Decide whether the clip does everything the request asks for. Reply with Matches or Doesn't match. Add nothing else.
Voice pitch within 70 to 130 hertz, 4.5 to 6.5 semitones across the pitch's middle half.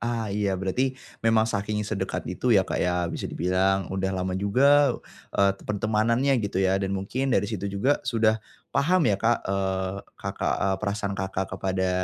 Doesn't match